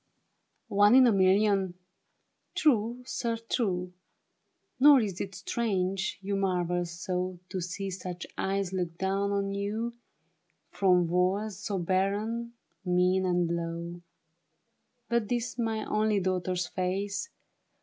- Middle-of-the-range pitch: No, high, 195 Hz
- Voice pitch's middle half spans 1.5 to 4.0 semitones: Yes, average, 2.9 semitones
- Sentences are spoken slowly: Yes, slow, 120 wpm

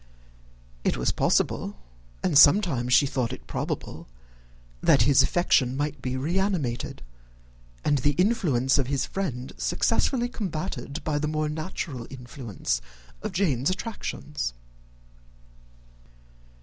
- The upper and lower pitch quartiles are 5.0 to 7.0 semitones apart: Yes, wide, 5.5 semitones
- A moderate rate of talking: No, slow, 115 wpm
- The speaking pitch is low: No, medium, 145 Hz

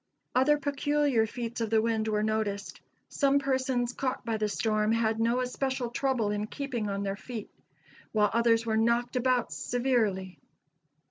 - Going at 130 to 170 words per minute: Yes, average, 155 wpm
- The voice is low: No, high, 230 Hz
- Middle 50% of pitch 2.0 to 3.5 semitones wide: Yes, average, 2.9 semitones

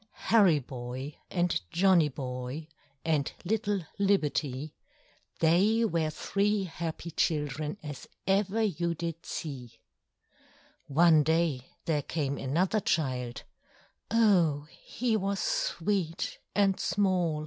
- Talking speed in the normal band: No, slow, 105 wpm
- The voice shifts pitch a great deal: No, average, 5.0 semitones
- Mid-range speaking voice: Yes, medium, 165 Hz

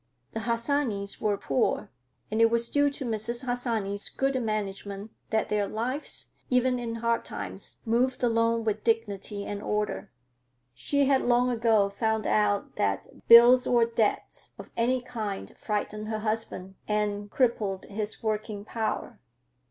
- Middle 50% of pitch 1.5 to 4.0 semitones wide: Yes, narrow, 2.5 semitones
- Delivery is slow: No, average, 145 wpm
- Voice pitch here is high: Yes, high, 220 Hz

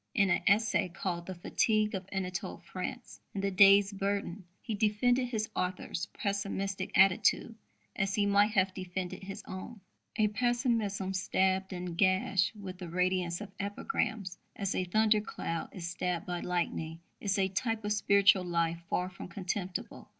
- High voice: Yes, high, 195 Hz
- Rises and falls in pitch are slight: Yes, narrow, 2.2 semitones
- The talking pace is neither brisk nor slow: Yes, average, 155 wpm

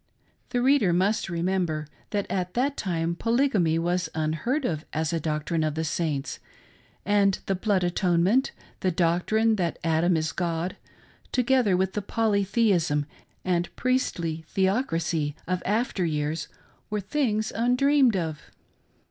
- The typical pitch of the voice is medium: Yes, medium, 180 Hz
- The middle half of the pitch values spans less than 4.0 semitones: No, average, 4.8 semitones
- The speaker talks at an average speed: No, slow, 130 wpm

